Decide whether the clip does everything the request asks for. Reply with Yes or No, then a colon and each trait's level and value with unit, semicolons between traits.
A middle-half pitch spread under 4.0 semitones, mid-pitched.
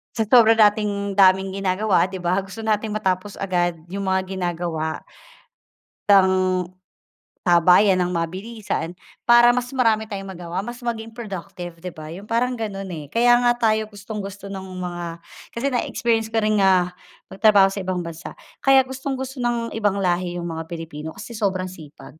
No: average, 3.6 semitones; high, 195 Hz